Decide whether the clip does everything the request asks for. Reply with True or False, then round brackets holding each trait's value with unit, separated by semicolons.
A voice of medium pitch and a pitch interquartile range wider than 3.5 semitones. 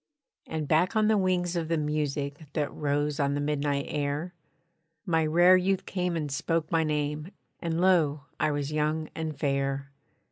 False (155 Hz; 2.8 semitones)